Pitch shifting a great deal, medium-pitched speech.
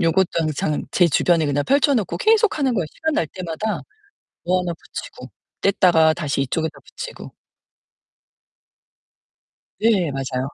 Yes: wide, 5.8 semitones; medium, 175 Hz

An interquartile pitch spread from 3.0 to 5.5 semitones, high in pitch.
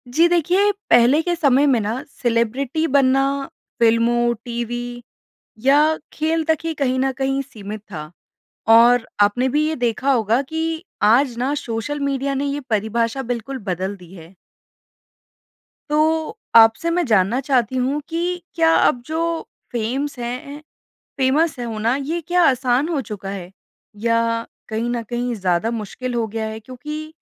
Yes: average, 4.2 semitones; very high, 250 Hz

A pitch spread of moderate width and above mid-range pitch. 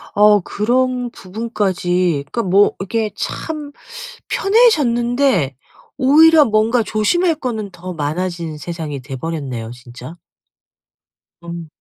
No: wide, 6.9 semitones; high, 205 Hz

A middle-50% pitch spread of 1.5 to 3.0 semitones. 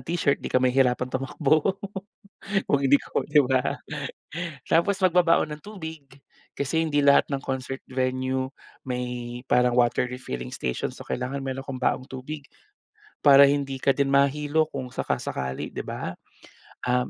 Yes: narrow, 2.5 semitones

